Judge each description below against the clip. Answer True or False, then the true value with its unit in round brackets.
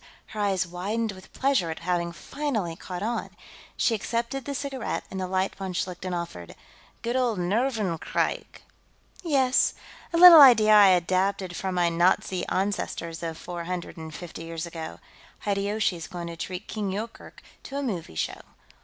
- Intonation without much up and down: False (4.8 semitones)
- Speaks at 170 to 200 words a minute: False (160 wpm)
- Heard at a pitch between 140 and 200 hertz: True (190 Hz)